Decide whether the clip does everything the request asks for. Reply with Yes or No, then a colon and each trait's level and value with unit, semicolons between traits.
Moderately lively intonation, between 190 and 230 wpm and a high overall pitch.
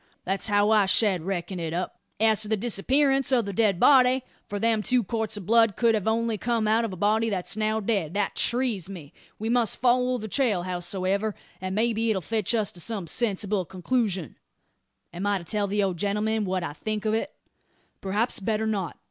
Yes: average, 3.0 semitones; average, 200 wpm; high, 210 Hz